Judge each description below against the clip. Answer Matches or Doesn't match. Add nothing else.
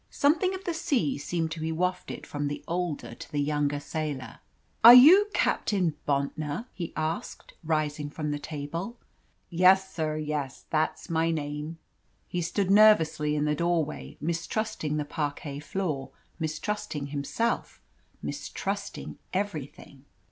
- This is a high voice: Doesn't match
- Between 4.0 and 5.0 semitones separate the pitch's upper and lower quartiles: Matches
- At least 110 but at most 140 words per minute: Matches